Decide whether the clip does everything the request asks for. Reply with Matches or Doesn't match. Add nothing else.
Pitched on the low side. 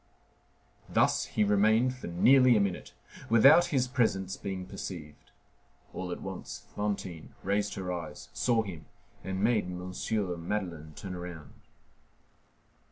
Matches